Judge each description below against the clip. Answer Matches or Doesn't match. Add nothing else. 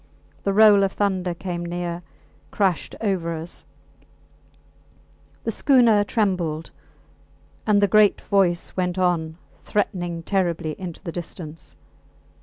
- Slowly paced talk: Matches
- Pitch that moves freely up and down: Doesn't match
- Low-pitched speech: Doesn't match